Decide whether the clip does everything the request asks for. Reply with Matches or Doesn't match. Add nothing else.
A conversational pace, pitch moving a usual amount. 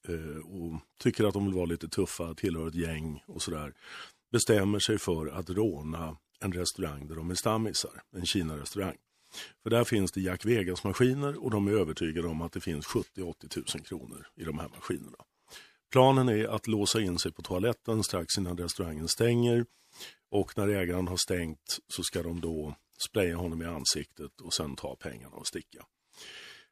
Matches